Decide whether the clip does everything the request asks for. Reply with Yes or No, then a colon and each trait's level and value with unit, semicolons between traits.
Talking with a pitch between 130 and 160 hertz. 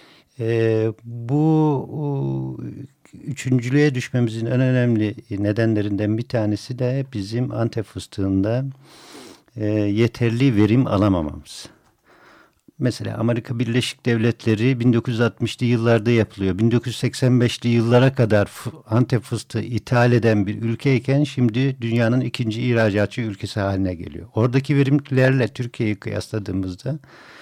No: low, 115 Hz